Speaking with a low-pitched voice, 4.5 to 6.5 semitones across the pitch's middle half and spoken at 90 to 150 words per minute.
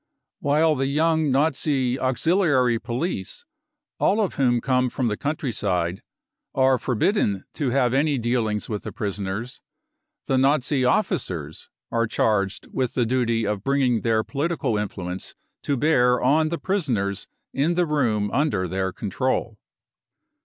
Yes: low, 125 Hz; average, 5.1 semitones; average, 140 wpm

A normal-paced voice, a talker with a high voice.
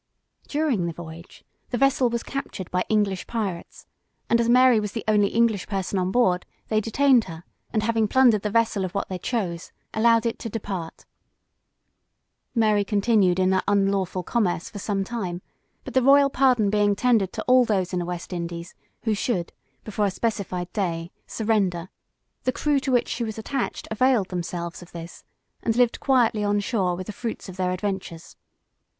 Yes: average, 180 wpm; high, 205 Hz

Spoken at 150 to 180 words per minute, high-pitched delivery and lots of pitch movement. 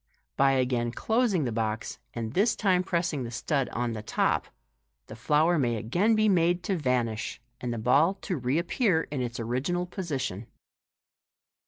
No: average, 160 wpm; medium, 140 Hz; wide, 6.8 semitones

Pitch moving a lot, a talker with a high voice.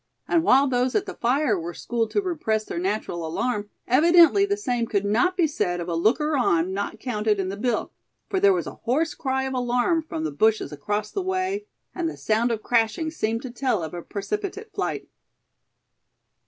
Yes: wide, 7.6 semitones; high, 245 Hz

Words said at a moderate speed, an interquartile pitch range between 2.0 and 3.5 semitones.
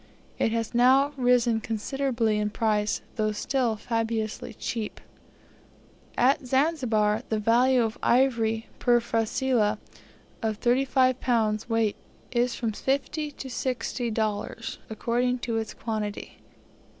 No: slow, 115 wpm; narrow, 2.5 semitones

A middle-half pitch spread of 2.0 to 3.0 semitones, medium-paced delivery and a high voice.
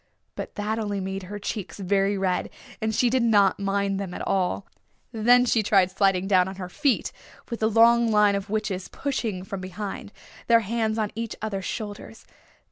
Yes: narrow, 2.5 semitones; average, 185 wpm; high, 205 Hz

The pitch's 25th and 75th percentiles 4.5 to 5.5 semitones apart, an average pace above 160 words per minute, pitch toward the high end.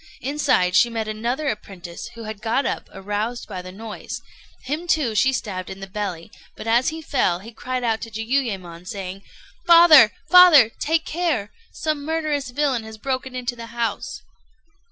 Yes: average, 5.2 semitones; average, 170 wpm; high, 230 Hz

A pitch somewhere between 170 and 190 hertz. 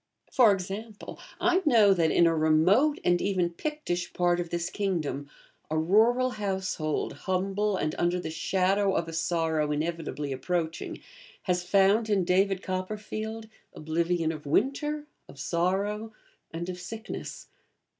Yes: medium, 185 Hz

